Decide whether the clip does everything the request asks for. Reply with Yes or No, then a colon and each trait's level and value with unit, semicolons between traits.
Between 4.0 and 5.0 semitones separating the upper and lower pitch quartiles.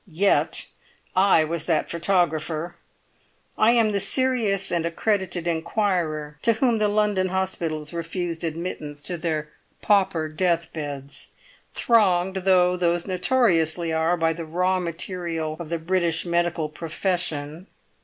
No: average, 2.8 semitones